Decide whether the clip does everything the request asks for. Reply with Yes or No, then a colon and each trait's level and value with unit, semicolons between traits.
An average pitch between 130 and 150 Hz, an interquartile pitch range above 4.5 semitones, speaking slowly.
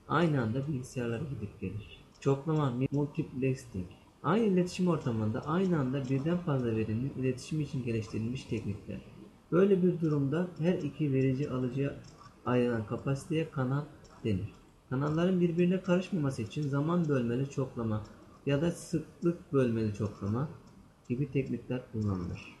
Yes: low, 135 Hz; average, 5.1 semitones; slow, 120 wpm